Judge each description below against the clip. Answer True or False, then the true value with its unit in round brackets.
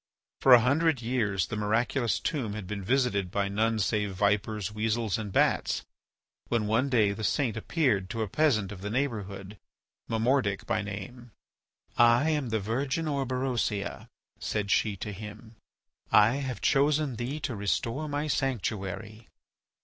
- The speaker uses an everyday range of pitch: True (4.1 semitones)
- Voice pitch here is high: False (110 Hz)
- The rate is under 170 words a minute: True (150 wpm)